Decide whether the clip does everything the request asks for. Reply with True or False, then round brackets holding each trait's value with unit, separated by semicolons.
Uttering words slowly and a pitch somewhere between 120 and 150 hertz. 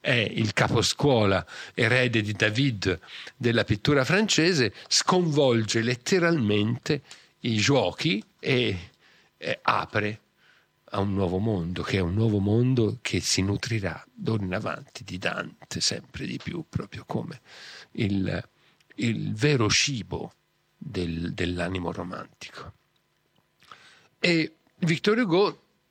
False (110 wpm; 110 Hz)